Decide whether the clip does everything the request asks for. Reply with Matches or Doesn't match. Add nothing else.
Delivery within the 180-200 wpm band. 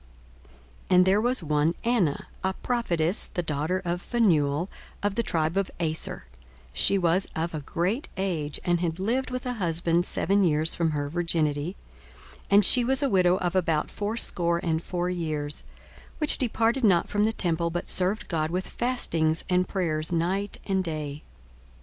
Doesn't match